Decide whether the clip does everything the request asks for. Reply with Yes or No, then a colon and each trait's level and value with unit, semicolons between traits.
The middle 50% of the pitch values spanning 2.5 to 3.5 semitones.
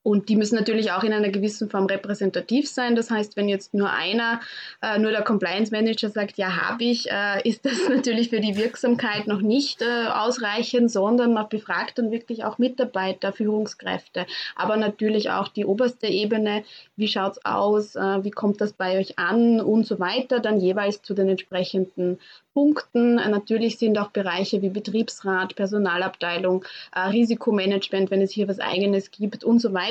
Yes: average, 2.8 semitones